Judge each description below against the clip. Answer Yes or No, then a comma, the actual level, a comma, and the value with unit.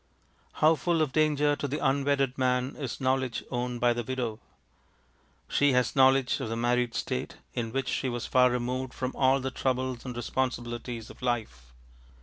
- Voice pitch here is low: Yes, low, 130 Hz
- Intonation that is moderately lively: No, narrow, 1.8 semitones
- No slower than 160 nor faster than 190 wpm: Yes, average, 170 wpm